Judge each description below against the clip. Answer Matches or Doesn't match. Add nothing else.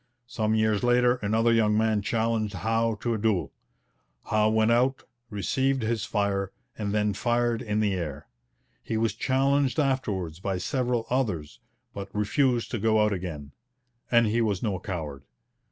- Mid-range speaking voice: Doesn't match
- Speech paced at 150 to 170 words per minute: Matches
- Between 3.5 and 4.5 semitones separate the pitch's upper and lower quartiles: Doesn't match